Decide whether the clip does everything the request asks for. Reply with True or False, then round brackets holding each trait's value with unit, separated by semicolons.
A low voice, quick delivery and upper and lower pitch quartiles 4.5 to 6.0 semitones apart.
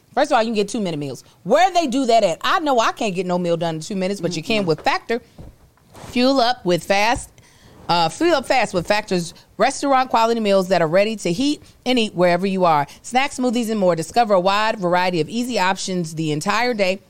False (200 Hz; 235 wpm; 5.6 semitones)